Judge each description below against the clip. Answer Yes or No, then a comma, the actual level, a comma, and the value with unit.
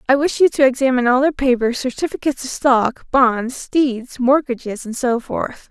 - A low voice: No, very high, 255 Hz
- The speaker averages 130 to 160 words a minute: No, average, 180 wpm